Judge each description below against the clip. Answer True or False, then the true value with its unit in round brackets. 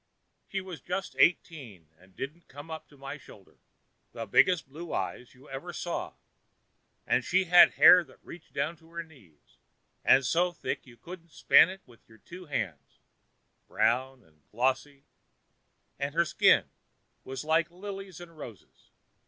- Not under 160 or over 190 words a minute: False (150 wpm)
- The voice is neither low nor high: True (150 Hz)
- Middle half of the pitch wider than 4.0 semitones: True (5.3 semitones)